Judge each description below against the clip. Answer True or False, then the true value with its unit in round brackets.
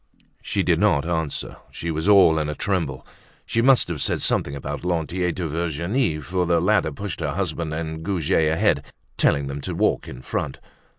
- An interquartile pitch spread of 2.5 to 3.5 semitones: True (2.9 semitones)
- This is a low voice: True (80 Hz)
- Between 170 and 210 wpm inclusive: True (185 wpm)